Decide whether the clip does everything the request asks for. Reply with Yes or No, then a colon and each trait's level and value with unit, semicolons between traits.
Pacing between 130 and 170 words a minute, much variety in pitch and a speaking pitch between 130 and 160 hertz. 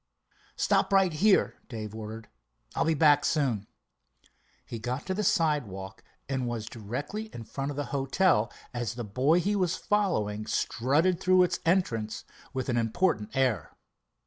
Yes: average, 150 wpm; wide, 7.5 semitones; low, 135 Hz